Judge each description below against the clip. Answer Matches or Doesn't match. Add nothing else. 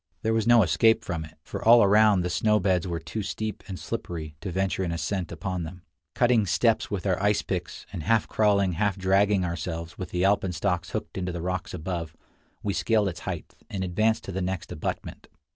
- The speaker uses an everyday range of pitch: Matches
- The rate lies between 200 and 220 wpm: Matches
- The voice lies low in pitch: Matches